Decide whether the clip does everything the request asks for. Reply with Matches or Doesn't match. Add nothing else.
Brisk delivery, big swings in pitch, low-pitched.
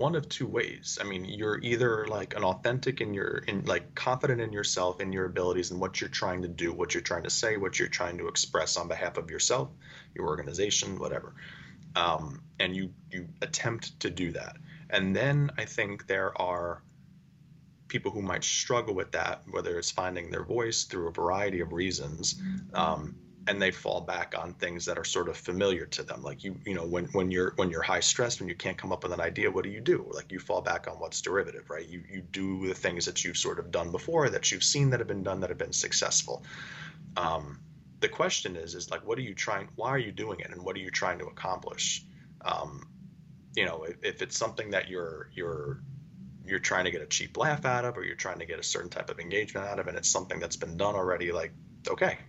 Matches